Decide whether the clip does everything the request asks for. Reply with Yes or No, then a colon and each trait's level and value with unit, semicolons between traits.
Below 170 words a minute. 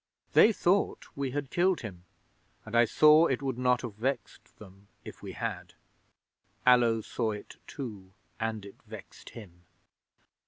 Yes: average, 150 wpm